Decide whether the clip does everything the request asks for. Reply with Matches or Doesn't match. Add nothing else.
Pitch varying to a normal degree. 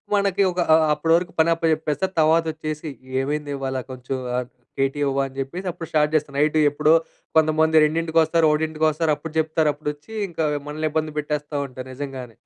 Doesn't match